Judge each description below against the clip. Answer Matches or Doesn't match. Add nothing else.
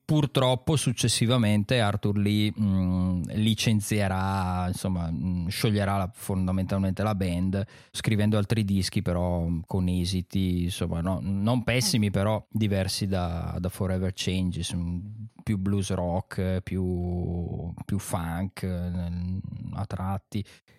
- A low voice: Matches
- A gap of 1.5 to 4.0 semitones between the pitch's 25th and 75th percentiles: Matches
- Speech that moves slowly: Matches